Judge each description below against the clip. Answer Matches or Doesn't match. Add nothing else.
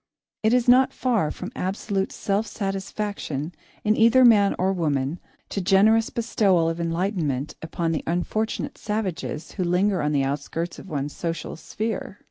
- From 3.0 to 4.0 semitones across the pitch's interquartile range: Doesn't match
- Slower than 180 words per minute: Matches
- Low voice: Doesn't match